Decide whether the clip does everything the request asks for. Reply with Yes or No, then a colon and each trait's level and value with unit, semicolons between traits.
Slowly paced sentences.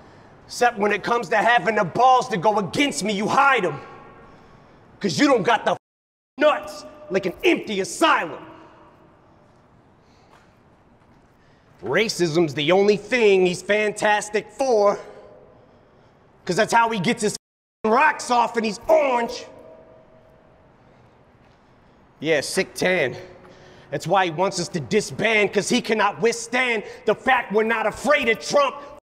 Yes: slow, 130 wpm